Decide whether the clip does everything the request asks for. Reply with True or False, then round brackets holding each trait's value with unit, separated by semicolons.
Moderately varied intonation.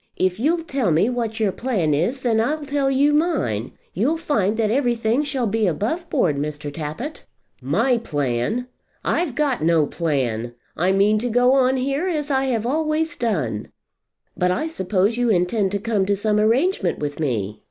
False (7.5 semitones)